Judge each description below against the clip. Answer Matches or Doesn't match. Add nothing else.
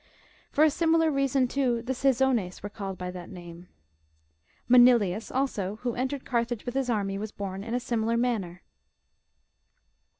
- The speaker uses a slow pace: Doesn't match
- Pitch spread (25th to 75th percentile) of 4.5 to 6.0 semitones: Matches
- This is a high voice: Matches